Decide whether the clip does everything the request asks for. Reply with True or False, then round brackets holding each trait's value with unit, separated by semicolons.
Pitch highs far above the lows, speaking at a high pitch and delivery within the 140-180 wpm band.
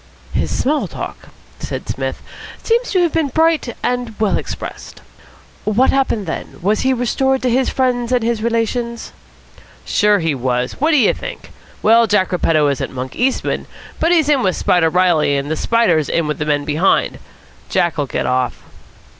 True (8.3 semitones; 225 Hz; 170 wpm)